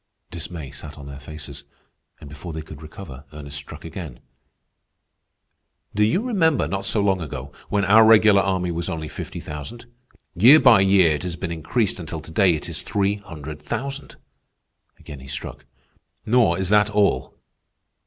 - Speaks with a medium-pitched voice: No, very low, 85 Hz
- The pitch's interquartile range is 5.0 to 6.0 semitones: Yes, wide, 5.4 semitones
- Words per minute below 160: No, average, 165 wpm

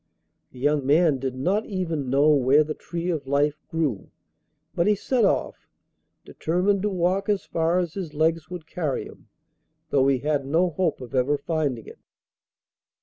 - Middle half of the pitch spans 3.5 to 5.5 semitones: Yes, average, 4.2 semitones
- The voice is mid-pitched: Yes, medium, 155 Hz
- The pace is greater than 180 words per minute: No, average, 170 wpm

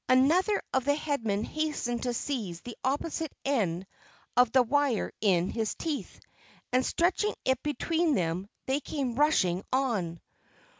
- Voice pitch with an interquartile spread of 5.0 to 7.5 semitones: Yes, wide, 5.5 semitones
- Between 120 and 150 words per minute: Yes, average, 140 wpm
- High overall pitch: Yes, very high, 260 Hz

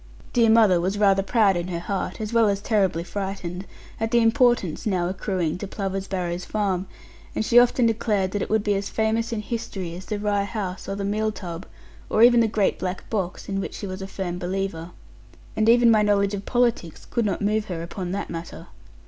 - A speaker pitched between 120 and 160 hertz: No, high, 200 Hz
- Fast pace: Yes, fast, 215 wpm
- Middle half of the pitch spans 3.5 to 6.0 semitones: No, average, 2.9 semitones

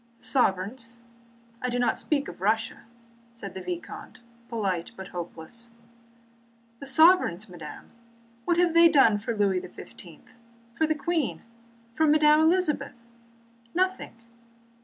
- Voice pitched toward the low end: No, high, 245 Hz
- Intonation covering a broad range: Yes, wide, 7.8 semitones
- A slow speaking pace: Yes, slow, 130 wpm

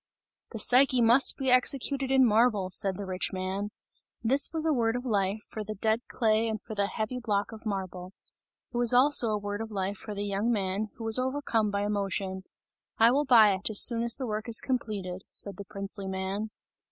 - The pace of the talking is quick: Yes, fast, 210 wpm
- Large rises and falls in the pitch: No, average, 3.3 semitones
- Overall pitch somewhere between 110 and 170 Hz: No, high, 215 Hz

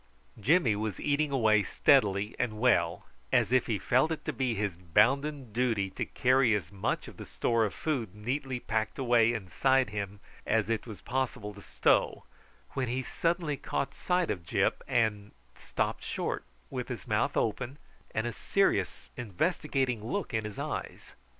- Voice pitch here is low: Yes, low, 115 Hz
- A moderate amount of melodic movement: Yes, average, 4.1 semitones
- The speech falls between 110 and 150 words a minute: No, average, 165 wpm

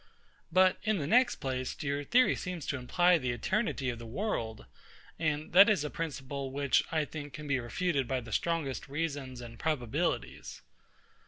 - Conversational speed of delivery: Yes, average, 170 wpm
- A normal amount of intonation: Yes, average, 4.8 semitones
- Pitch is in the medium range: Yes, medium, 145 Hz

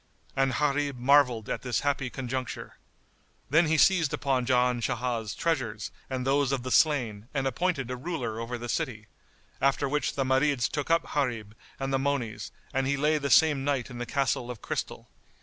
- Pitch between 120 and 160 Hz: Yes, low, 135 Hz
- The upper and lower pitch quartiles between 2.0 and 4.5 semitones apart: Yes, average, 2.8 semitones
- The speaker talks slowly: No, average, 185 wpm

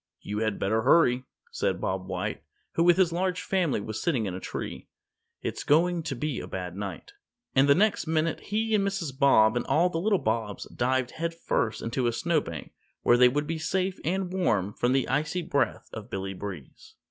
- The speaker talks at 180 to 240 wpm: Yes, average, 195 wpm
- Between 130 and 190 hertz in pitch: Yes, medium, 140 Hz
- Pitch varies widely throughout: Yes, wide, 7.8 semitones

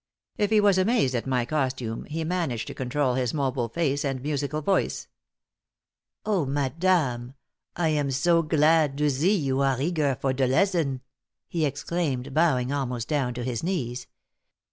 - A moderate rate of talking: Yes, average, 160 wpm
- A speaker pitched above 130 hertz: Yes, medium, 140 Hz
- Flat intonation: No, average, 4.1 semitones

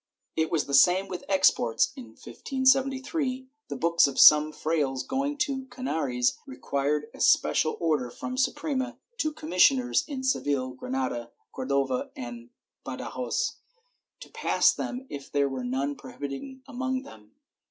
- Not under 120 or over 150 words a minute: Yes, average, 145 wpm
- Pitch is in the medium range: Yes, medium, 160 Hz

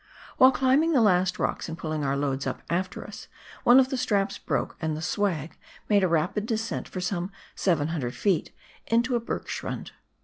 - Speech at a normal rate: Yes, average, 180 wpm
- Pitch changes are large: Yes, wide, 6.2 semitones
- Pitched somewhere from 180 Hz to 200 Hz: Yes, medium, 185 Hz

